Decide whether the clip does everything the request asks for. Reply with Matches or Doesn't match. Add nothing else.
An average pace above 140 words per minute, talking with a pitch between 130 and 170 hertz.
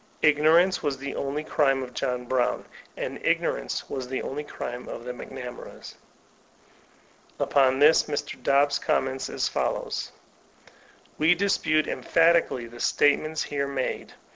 Doesn't match